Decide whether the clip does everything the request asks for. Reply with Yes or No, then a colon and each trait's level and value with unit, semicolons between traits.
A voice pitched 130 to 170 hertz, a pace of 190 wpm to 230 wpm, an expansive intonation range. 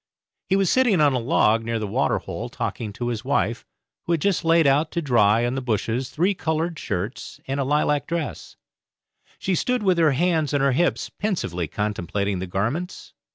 Yes: medium, 140 Hz; average, 195 wpm; wide, 6.9 semitones